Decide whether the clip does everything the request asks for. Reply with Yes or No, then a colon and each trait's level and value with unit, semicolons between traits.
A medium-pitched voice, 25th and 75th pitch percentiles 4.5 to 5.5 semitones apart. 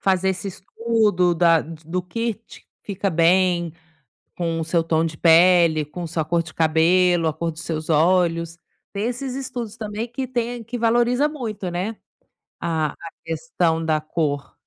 Yes: medium, 175 Hz; average, 4.8 semitones